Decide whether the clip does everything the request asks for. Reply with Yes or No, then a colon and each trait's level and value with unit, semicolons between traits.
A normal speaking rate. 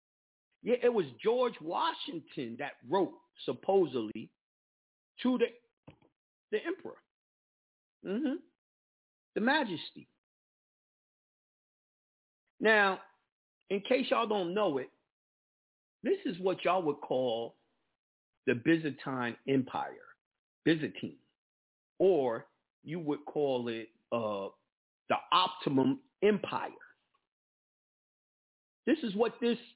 No: slow, 90 wpm